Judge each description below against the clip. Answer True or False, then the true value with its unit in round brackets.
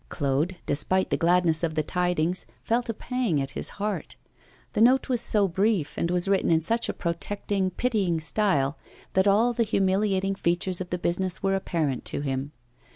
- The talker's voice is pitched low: False (185 Hz)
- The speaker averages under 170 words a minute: False (180 wpm)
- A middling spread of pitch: True (3.7 semitones)